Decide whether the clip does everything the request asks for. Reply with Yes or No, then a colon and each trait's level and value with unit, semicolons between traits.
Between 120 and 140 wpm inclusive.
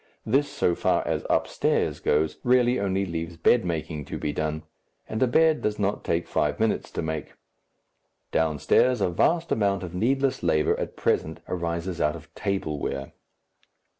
No: average, 160 wpm